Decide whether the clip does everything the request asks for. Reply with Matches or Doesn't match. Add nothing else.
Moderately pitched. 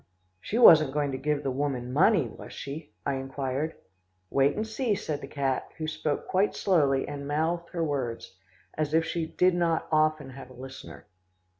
Matches